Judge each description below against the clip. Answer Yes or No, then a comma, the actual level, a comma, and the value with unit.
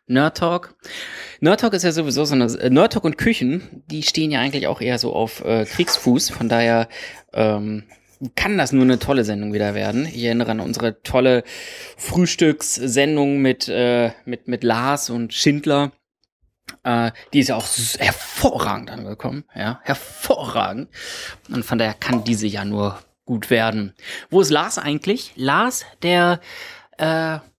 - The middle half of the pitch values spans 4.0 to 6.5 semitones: Yes, average, 4.7 semitones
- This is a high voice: No, low, 125 Hz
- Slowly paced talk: No, average, 160 wpm